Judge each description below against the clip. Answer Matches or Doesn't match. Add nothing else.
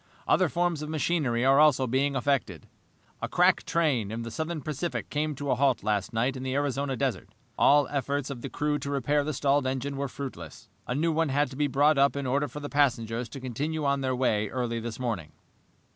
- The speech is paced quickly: Matches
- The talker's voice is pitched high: Doesn't match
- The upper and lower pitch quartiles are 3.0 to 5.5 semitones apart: Doesn't match